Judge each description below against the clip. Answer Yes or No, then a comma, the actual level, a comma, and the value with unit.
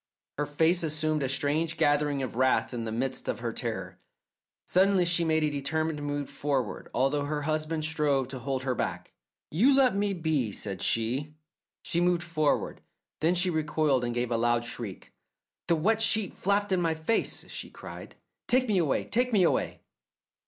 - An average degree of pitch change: Yes, average, 4.3 semitones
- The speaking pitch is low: No, medium, 155 Hz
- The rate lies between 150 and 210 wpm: Yes, average, 180 wpm